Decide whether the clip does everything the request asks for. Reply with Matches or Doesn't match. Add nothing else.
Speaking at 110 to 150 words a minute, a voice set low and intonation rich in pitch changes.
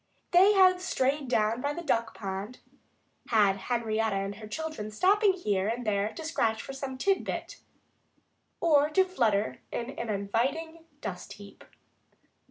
Doesn't match